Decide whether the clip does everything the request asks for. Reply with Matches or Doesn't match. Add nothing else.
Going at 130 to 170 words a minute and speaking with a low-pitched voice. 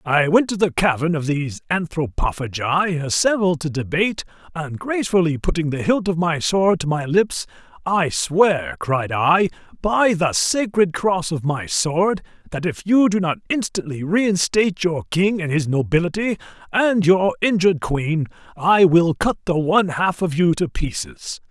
Doesn't match